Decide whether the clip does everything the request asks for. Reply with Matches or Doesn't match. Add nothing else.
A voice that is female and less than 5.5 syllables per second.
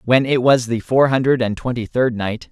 Doesn't match